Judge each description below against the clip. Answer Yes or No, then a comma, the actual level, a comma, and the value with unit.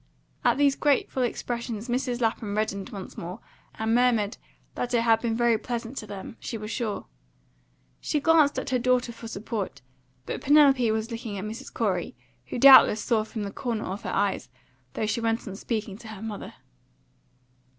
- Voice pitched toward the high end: Yes, high, 230 Hz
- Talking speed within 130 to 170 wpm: No, average, 180 wpm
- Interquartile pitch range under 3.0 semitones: Yes, narrow, 2.6 semitones